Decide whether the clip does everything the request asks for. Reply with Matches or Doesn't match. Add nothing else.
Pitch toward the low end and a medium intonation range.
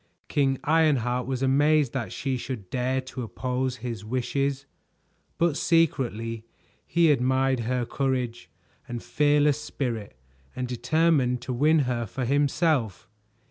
Matches